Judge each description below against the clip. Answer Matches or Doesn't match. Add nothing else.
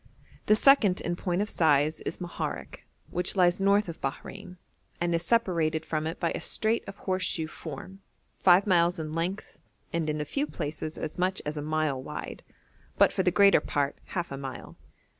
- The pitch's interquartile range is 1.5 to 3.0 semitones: Doesn't match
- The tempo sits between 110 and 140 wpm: Doesn't match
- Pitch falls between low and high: Matches